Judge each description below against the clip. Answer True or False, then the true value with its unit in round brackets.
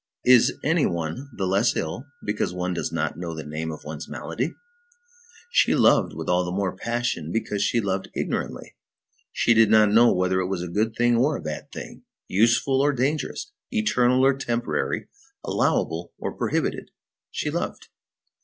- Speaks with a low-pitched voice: True (105 Hz)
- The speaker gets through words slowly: False (170 wpm)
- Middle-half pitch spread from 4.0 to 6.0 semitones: True (5.6 semitones)